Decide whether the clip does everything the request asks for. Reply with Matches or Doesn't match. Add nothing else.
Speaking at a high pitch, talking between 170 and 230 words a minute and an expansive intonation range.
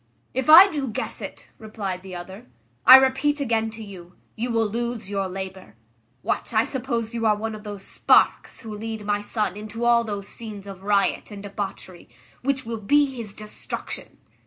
Doesn't match